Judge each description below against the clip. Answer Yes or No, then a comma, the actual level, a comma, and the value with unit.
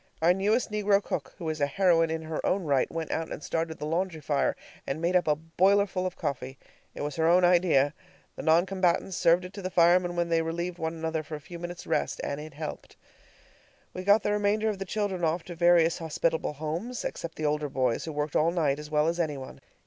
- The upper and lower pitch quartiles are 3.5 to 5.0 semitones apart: No, average, 2.8 semitones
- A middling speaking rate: No, fast, 235 wpm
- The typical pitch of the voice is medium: Yes, medium, 165 Hz